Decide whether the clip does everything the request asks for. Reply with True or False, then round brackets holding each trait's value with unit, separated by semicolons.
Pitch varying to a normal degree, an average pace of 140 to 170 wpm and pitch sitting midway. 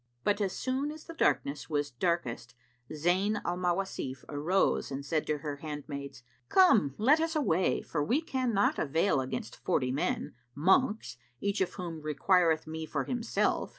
False (6.1 semitones; 155 wpm; 165 Hz)